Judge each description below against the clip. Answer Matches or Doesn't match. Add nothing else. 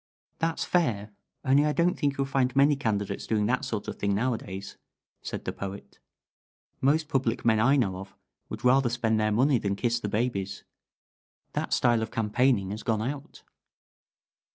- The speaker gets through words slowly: Doesn't match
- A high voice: Doesn't match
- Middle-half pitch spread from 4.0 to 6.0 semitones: Matches